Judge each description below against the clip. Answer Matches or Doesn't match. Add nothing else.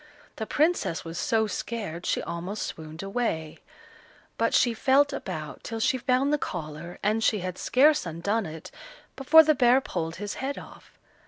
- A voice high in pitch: Matches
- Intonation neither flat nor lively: Doesn't match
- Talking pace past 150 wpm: Matches